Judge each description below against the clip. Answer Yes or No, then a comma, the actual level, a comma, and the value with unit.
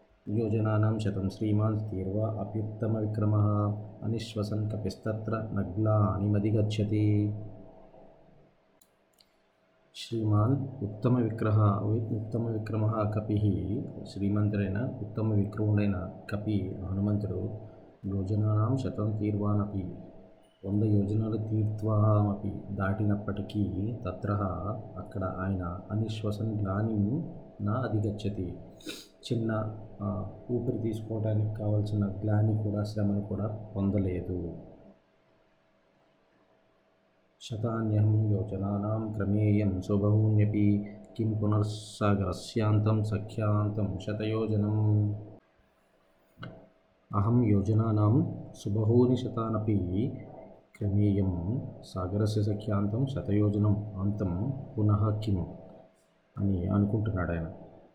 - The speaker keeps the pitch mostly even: Yes, narrow, 1.5 semitones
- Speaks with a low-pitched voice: Yes, low, 105 Hz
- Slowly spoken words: Yes, slow, 65 wpm